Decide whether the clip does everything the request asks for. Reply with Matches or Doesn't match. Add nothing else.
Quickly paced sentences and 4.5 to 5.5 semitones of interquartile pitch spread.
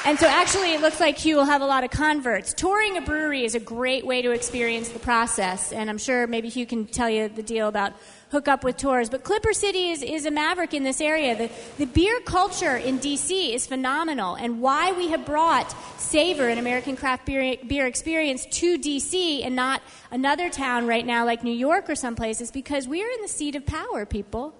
Matches